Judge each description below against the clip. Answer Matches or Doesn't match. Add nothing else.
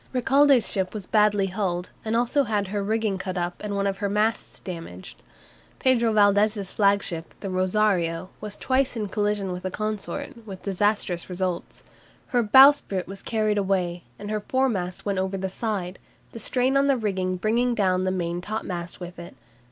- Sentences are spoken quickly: Doesn't match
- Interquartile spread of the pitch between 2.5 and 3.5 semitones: Matches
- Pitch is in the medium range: Doesn't match